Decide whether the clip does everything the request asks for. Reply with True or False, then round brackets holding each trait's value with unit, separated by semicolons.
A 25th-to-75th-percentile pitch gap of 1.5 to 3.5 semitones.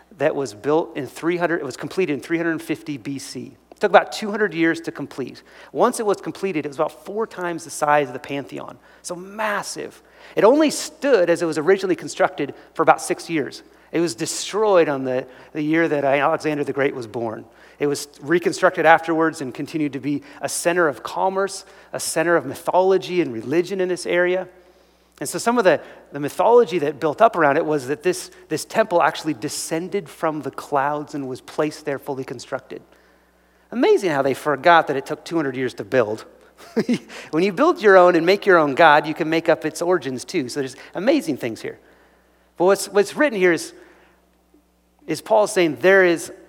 False (4.1 semitones)